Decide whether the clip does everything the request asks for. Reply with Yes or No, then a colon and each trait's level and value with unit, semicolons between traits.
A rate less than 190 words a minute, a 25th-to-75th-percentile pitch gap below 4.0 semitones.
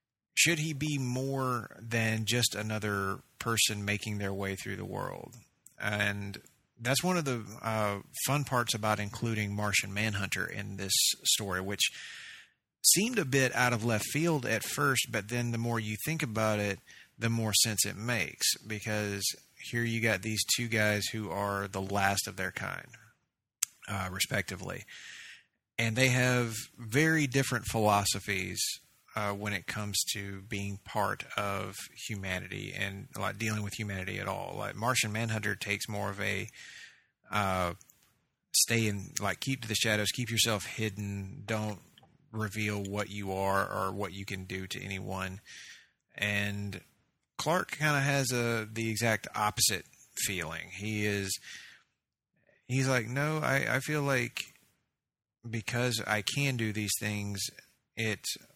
Yes: average, 150 wpm; average, 3.3 semitones